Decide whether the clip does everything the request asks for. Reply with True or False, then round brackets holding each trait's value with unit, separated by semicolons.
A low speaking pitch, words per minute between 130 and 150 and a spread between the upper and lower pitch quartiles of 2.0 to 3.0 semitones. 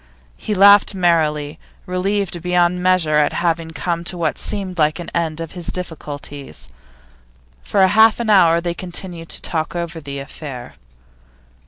False (170 Hz; 145 wpm; 2.6 semitones)